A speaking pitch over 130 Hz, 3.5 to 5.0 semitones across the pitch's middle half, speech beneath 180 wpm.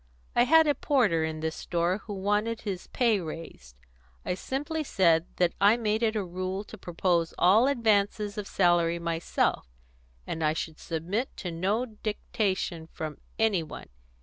Yes: high, 190 Hz; average, 4.7 semitones; average, 160 wpm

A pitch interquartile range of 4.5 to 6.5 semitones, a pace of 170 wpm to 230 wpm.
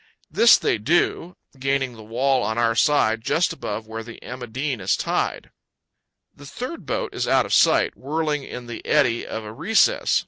Yes: average, 4.9 semitones; average, 180 wpm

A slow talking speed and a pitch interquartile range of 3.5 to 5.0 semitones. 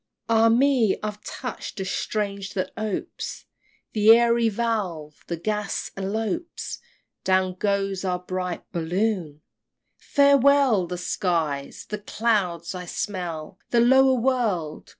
Yes: slow, 120 wpm; average, 4.2 semitones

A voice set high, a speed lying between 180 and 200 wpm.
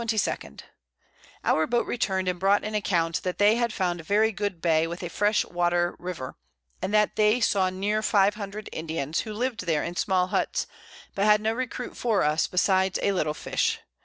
Yes: high, 195 Hz; average, 190 wpm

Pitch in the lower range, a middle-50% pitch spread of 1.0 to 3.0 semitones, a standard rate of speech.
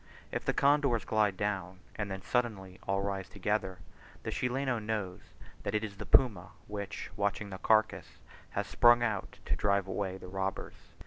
Yes: low, 100 Hz; narrow, 2.5 semitones; average, 170 wpm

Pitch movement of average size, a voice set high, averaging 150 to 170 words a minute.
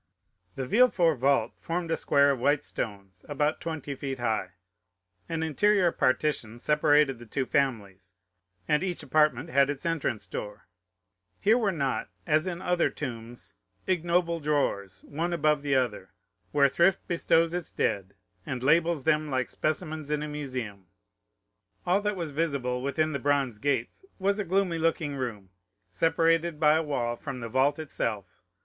No: average, 4.6 semitones; medium, 145 Hz; average, 155 wpm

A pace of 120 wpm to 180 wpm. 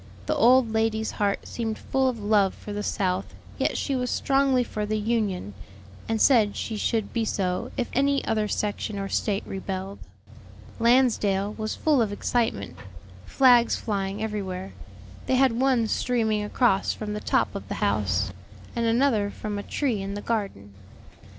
Yes: average, 165 wpm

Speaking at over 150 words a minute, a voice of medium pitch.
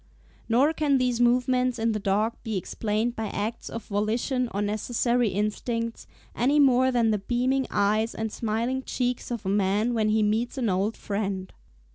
No: average, 170 wpm; high, 230 Hz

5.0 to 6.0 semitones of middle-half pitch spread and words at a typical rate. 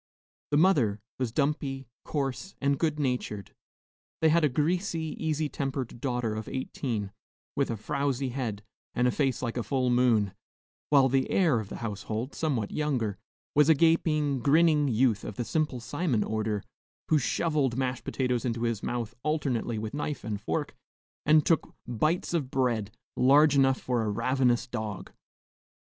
No: average, 4.3 semitones; average, 160 wpm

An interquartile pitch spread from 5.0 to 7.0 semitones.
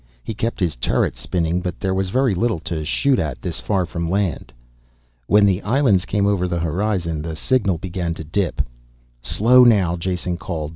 No: average, 3.4 semitones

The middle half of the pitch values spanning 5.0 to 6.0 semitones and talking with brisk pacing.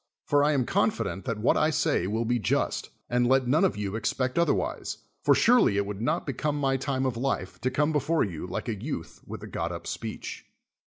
Yes: wide, 5.4 semitones; fast, 220 wpm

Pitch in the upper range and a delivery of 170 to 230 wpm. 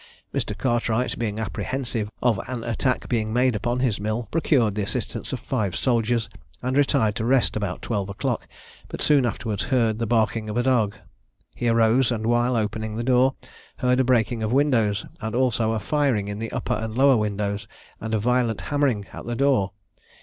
No: low, 115 Hz; average, 185 wpm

